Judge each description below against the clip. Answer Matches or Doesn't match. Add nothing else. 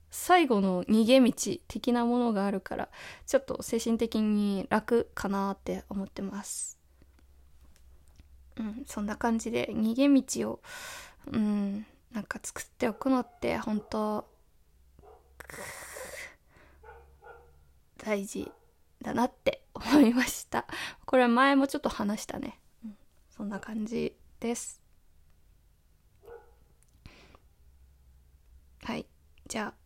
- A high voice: Matches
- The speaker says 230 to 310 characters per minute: Doesn't match